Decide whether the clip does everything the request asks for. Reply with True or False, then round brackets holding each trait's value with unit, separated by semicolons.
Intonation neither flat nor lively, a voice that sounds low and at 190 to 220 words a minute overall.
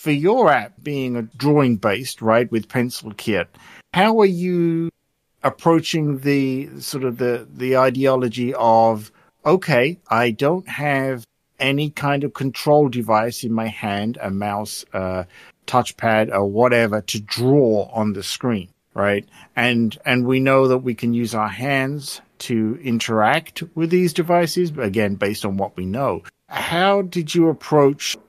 False (4.7 semitones; 125 Hz; 150 wpm)